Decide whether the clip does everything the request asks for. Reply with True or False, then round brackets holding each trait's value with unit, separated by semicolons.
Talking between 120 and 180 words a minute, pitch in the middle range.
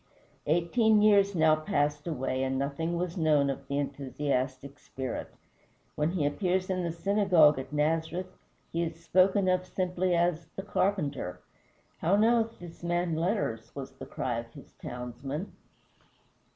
True (145 wpm; 165 Hz)